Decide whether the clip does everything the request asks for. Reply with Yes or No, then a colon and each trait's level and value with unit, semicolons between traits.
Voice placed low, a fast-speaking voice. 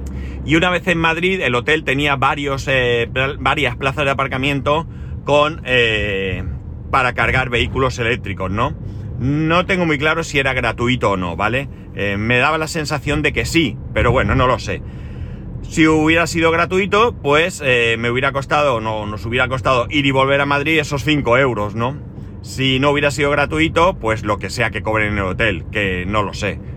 Yes: low, 130 Hz; fast, 195 wpm